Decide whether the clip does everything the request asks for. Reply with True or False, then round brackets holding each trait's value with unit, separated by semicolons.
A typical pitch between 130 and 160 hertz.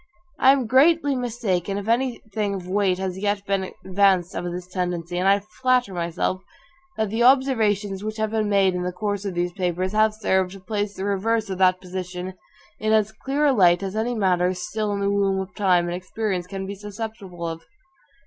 False (200 Hz)